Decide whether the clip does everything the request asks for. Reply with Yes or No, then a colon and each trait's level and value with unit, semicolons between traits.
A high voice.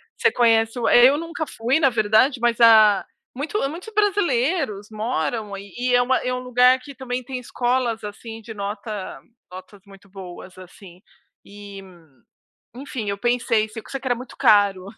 Yes: high, 235 Hz